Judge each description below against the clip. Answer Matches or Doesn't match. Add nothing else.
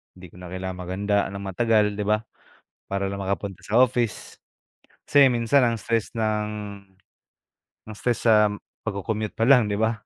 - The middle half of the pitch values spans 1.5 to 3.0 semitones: Matches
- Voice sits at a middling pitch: Doesn't match